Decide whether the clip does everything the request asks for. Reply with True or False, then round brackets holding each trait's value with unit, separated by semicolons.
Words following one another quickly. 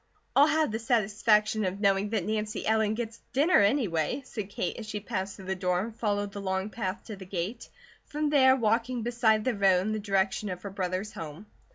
True (210 wpm)